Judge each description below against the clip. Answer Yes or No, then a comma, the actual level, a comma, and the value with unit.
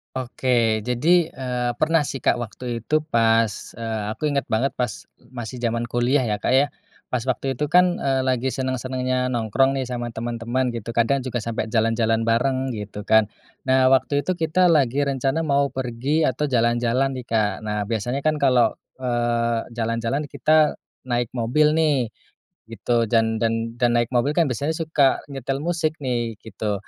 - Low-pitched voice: Yes, low, 125 Hz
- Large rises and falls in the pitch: No, average, 3.0 semitones